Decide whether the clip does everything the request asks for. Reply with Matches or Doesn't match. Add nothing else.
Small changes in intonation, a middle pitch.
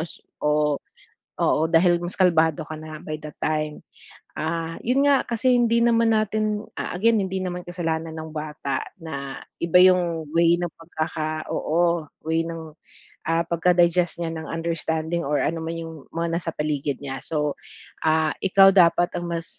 Matches